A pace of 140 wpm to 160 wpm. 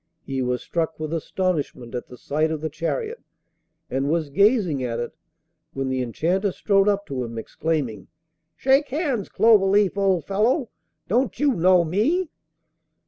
Yes: average, 150 wpm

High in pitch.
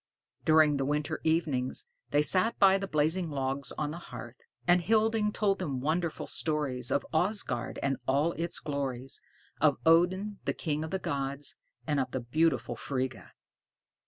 No: medium, 150 Hz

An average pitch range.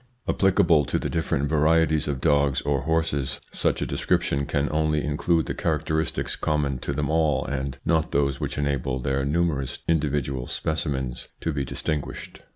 No: narrow, 2.3 semitones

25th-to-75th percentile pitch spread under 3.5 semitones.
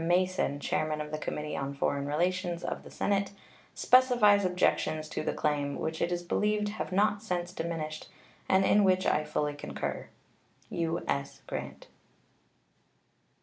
No: average, 4.3 semitones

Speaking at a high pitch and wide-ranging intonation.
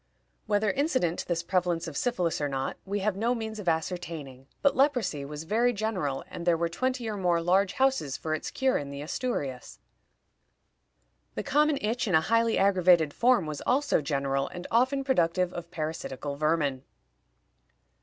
No: medium, 180 Hz; wide, 6.8 semitones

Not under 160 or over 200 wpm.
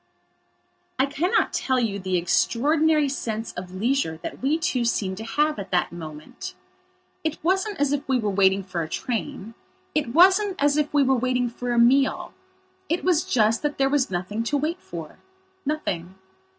Yes: average, 175 wpm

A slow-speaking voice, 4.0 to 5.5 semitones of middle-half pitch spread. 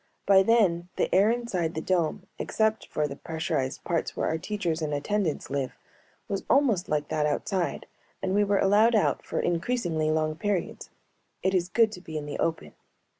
No: average, 180 wpm; average, 4.6 semitones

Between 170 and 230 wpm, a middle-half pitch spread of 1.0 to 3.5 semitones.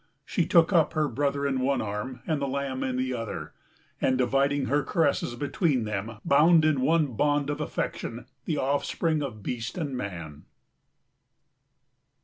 No: average, 155 wpm; average, 3.0 semitones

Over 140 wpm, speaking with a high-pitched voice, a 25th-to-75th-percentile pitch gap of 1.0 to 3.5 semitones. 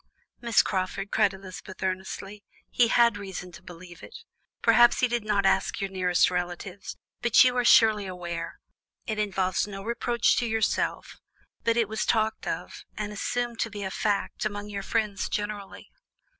Yes: average, 165 wpm; high, 205 Hz; average, 2.8 semitones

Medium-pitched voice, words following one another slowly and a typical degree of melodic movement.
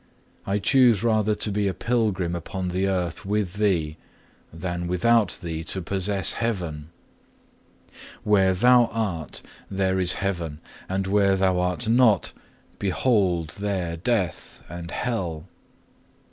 No: very low, 95 Hz; slow, 125 wpm; average, 3.2 semitones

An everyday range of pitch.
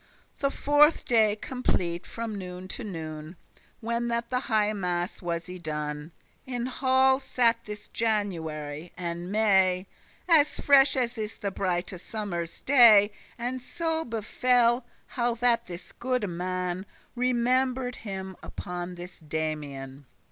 No: wide, 5.8 semitones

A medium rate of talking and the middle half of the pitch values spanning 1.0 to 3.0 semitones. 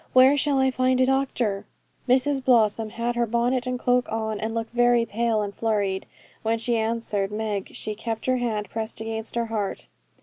Yes: average, 190 wpm; narrow, 2.4 semitones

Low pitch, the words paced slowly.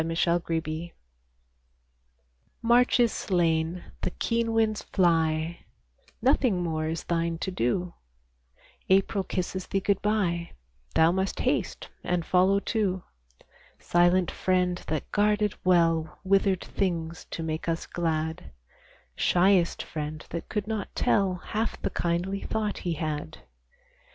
No: medium, 180 Hz; slow, 130 wpm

